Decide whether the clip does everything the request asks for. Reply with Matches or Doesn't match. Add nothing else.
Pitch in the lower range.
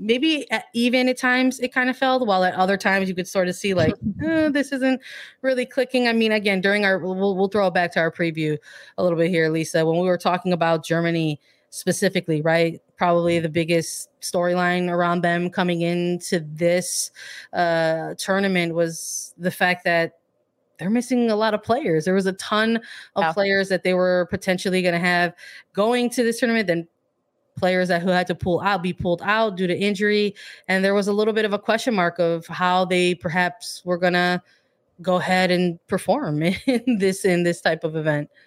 Doesn't match